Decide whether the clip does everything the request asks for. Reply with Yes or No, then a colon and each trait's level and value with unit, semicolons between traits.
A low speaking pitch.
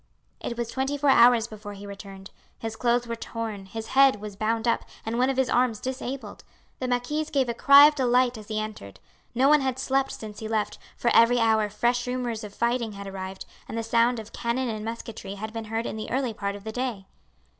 No: high, 230 Hz